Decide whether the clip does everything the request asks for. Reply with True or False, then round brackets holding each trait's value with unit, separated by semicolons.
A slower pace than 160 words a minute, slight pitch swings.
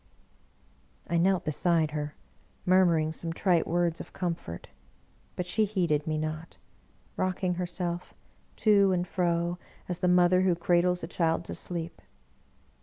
True (140 wpm; 1.8 semitones)